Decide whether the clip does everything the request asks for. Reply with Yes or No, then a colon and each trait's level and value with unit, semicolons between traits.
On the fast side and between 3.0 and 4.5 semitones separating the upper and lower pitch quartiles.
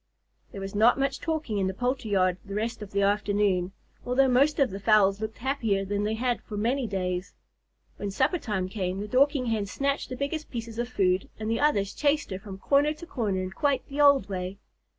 No: fast, 215 wpm; wide, 5.4 semitones